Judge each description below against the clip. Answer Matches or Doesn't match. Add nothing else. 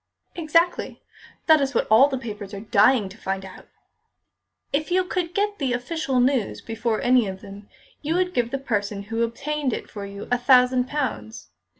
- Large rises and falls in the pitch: Matches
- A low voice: Doesn't match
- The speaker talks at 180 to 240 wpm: Matches